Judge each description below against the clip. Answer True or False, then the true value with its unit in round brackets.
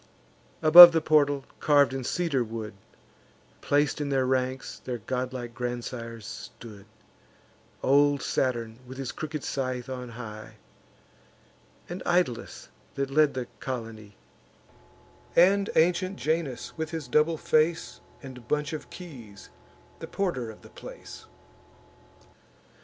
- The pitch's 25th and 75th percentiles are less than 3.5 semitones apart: False (4.2 semitones)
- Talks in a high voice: False (135 Hz)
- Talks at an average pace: False (120 wpm)